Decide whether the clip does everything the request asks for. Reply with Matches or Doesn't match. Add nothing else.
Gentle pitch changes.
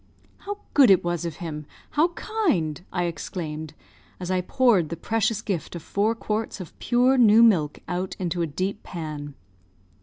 Doesn't match